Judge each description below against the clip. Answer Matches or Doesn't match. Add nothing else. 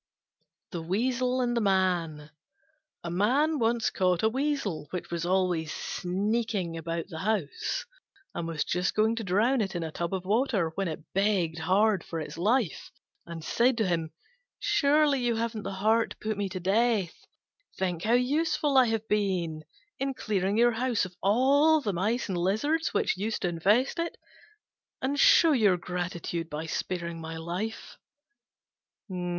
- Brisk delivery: Doesn't match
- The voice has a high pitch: Matches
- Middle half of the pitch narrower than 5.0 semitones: Doesn't match